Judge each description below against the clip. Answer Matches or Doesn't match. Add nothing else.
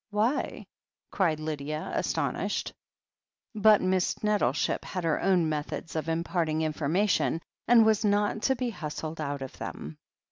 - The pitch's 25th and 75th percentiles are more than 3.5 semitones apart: Matches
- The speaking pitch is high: Doesn't match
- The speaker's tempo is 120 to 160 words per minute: Matches